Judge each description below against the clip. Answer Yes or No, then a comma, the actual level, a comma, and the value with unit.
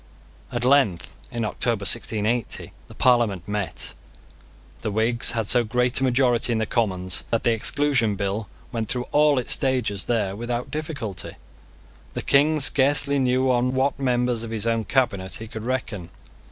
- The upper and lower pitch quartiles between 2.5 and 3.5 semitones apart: Yes, average, 3.0 semitones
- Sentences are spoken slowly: No, average, 160 wpm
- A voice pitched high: No, low, 120 Hz